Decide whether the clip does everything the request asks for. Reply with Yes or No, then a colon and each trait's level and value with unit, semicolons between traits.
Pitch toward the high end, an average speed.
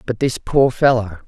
No: low, 120 Hz; average, 190 wpm